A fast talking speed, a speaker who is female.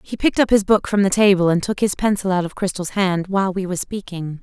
Yes: fast, 270 wpm; female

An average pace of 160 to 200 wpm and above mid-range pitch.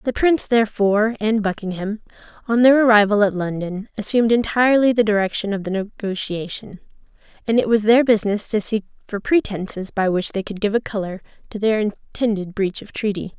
Yes: average, 175 wpm; high, 210 Hz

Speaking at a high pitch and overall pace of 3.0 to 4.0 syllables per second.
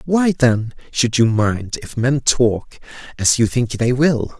No: low, 125 Hz; 3.6 syllables/s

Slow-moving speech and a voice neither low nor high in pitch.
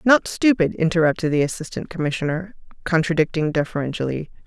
Yes: slow, 110 wpm; medium, 165 Hz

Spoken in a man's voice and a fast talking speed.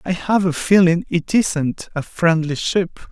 No: male; average, 175 wpm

